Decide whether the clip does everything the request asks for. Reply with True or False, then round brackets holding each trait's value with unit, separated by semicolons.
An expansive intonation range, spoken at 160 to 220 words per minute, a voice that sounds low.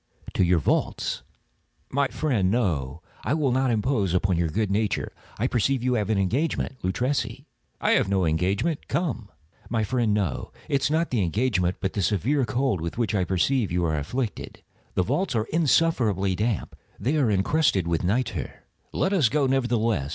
True (6.1 semitones; 175 wpm; 110 Hz)